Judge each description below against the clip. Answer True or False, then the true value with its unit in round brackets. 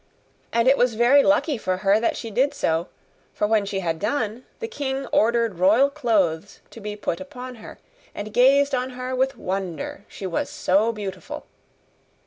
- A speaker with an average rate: True (175 wpm)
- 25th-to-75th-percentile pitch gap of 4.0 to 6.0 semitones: True (4.7 semitones)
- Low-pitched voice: False (225 Hz)